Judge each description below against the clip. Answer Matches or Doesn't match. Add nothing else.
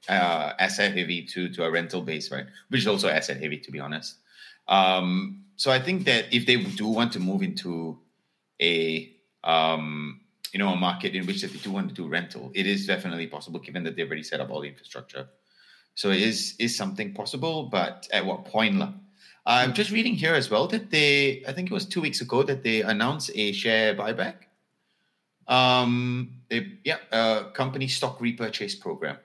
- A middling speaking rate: Matches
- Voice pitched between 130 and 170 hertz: Doesn't match